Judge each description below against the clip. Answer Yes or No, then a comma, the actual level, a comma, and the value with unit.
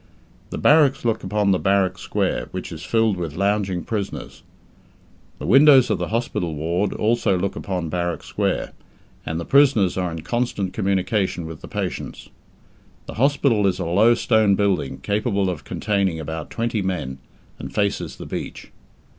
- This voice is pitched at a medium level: No, low, 100 Hz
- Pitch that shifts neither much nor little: Yes, average, 4.0 semitones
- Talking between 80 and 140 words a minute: No, average, 160 wpm